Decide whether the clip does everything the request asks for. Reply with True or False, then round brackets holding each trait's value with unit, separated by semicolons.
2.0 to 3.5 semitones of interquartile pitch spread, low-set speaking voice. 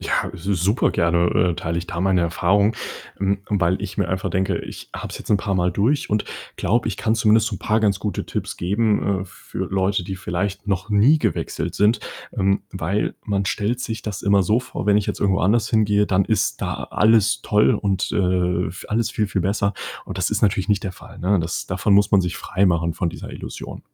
True (2.4 semitones; 100 Hz)